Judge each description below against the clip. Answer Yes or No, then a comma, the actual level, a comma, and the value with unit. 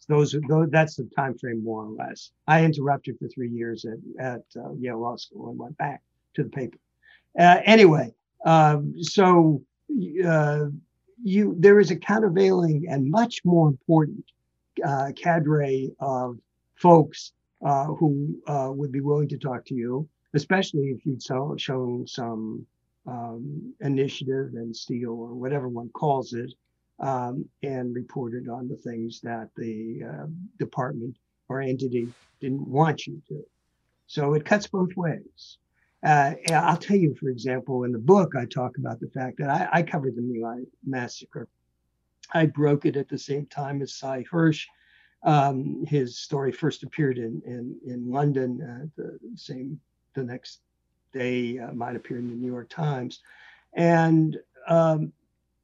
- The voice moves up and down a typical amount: Yes, average, 4.2 semitones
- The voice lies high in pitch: No, low, 135 Hz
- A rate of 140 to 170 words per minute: Yes, average, 160 wpm